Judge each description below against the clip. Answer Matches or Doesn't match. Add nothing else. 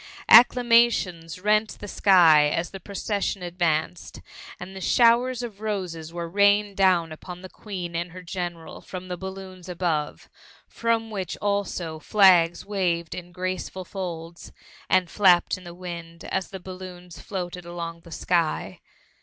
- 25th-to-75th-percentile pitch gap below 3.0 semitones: Matches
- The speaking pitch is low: Doesn't match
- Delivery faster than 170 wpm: Doesn't match